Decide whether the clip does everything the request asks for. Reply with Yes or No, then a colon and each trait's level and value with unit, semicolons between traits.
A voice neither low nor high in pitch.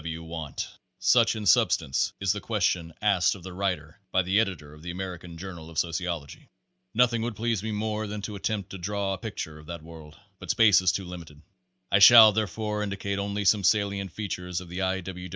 No: very low, 95 Hz